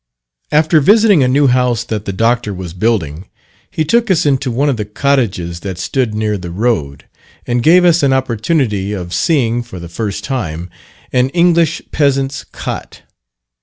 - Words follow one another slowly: No, average, 165 wpm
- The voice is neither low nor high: No, low, 120 Hz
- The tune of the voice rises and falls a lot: Yes, wide, 6.1 semitones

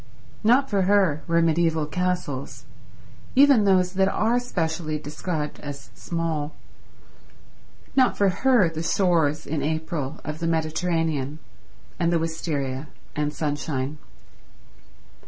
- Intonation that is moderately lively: Yes, average, 3.4 semitones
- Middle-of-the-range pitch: Yes, medium, 165 Hz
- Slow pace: Yes, slow, 115 wpm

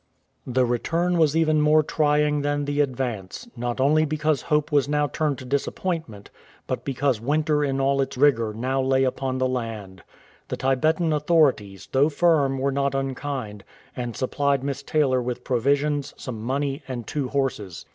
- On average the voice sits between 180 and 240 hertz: No, medium, 140 Hz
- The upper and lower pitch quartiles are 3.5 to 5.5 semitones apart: No, average, 2.8 semitones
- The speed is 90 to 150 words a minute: No, average, 165 wpm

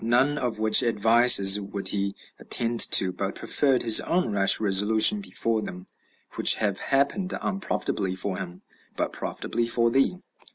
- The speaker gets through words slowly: No, average, 150 wpm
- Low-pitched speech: Yes, low, 110 Hz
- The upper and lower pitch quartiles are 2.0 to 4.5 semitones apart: Yes, average, 3.9 semitones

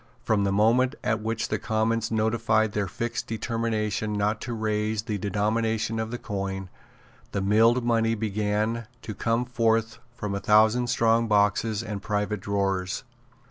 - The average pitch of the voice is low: Yes, low, 110 Hz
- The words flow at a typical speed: Yes, average, 150 wpm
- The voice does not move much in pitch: Yes, narrow, 1.7 semitones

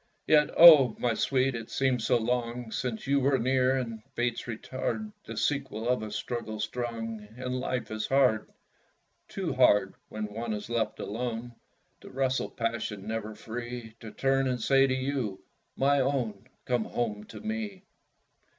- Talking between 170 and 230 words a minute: No, average, 160 wpm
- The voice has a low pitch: Yes, low, 120 Hz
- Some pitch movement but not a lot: Yes, average, 3.0 semitones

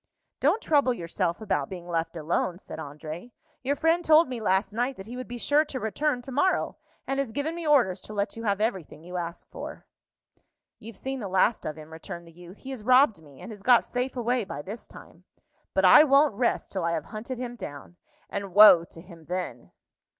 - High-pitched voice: Yes, high, 215 Hz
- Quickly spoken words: Yes, fast, 215 wpm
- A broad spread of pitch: Yes, wide, 6.6 semitones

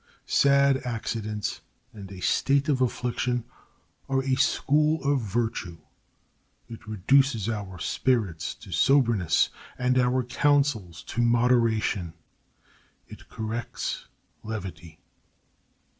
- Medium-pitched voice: No, low, 120 Hz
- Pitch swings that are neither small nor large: Yes, average, 4.1 semitones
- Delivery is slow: Yes, slow, 100 wpm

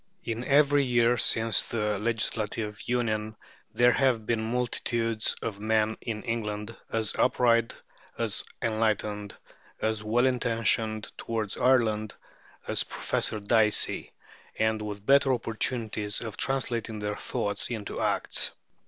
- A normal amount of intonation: No, narrow, 1.9 semitones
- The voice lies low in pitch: Yes, low, 110 Hz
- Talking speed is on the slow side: Yes, slow, 120 wpm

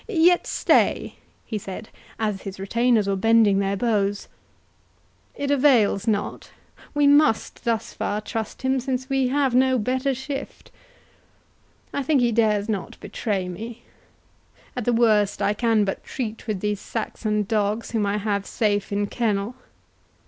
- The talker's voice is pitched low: No, high, 220 Hz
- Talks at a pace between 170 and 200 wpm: No, average, 140 wpm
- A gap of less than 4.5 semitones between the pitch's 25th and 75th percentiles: Yes, average, 3.7 semitones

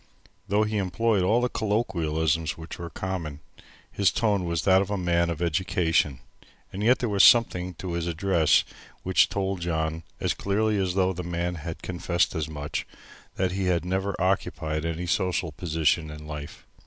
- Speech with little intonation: No, average, 3.0 semitones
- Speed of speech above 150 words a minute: Yes, average, 175 wpm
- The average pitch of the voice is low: Yes, very low, 90 Hz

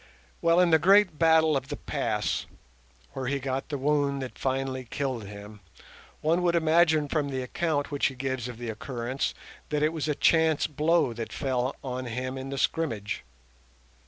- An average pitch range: Yes, average, 3.6 semitones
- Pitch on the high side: No, medium, 140 Hz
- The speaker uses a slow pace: No, average, 180 wpm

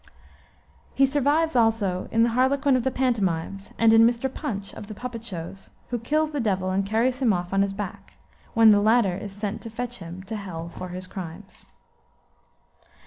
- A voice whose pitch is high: Yes, high, 220 Hz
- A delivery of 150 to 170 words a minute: No, average, 195 wpm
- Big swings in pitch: No, average, 4.2 semitones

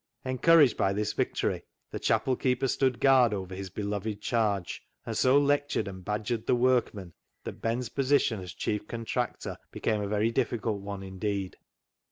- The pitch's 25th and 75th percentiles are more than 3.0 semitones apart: Yes, average, 4.0 semitones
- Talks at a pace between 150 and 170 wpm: Yes, average, 160 wpm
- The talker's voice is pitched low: Yes, low, 110 Hz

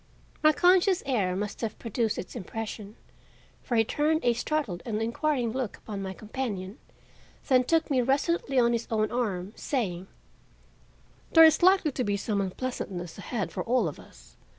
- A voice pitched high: Yes, high, 235 Hz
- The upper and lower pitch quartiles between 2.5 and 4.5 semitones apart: No, average, 5.0 semitones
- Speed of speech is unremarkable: Yes, average, 165 wpm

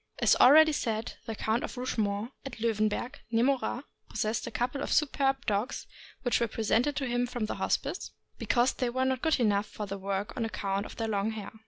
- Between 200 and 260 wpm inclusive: Yes, fast, 205 wpm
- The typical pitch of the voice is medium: No, high, 235 Hz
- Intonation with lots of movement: No, average, 3.3 semitones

